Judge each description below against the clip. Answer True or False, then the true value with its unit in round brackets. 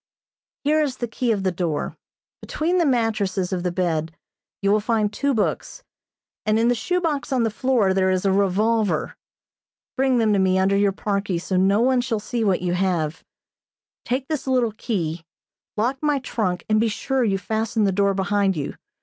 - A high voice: True (210 Hz)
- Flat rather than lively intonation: False (4.5 semitones)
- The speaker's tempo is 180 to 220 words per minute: True (190 wpm)